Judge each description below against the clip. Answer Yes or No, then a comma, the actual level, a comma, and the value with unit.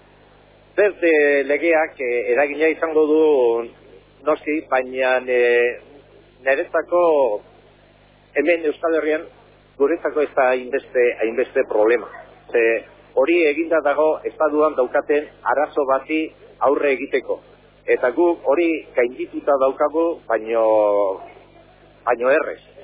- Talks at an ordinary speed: No, slow, 85 wpm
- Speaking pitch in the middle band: Yes, medium, 155 Hz